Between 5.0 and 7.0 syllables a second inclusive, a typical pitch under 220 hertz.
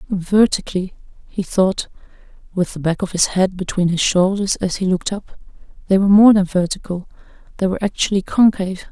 Yes: 5.8 syllables/s; high, 190 Hz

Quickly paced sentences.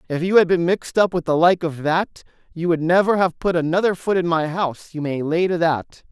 Yes: fast, 255 wpm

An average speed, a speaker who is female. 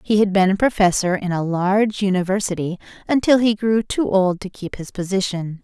Yes: average, 190 wpm; female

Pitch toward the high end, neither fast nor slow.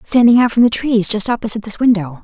No: high, 220 Hz; fast, 240 wpm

